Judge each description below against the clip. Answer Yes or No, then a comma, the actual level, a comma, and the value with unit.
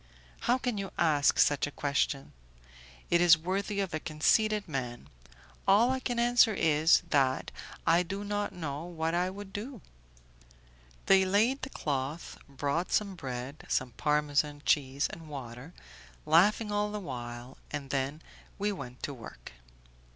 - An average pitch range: No, wide, 6.2 semitones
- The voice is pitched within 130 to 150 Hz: No, medium, 160 Hz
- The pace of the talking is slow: No, average, 150 wpm